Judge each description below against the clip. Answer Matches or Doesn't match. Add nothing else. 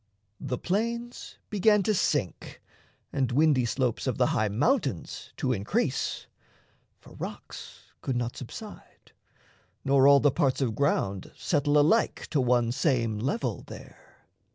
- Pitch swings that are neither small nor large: Matches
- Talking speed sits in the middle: Doesn't match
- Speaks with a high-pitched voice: Doesn't match